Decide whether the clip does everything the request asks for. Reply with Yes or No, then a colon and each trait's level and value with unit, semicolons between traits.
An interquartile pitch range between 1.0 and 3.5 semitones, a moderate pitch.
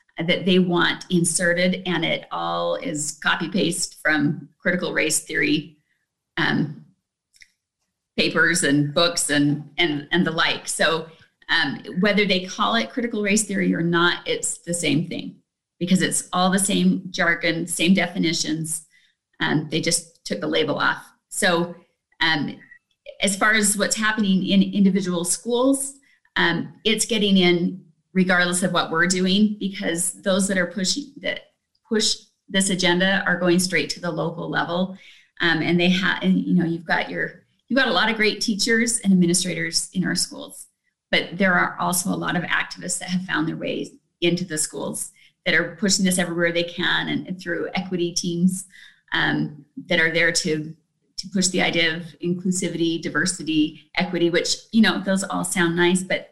Yes: average, 2.7 semitones; medium, 180 Hz